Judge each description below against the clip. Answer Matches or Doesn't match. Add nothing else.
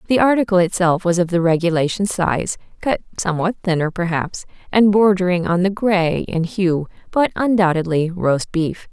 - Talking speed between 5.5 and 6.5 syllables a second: Doesn't match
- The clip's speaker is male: Doesn't match